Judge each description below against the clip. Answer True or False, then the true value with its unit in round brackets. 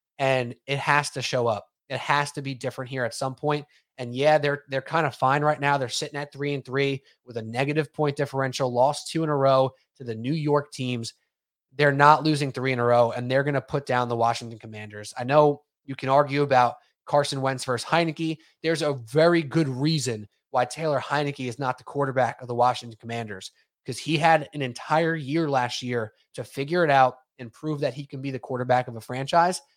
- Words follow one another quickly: True (220 wpm)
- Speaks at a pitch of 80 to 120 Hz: False (135 Hz)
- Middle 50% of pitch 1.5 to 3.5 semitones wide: True (2.8 semitones)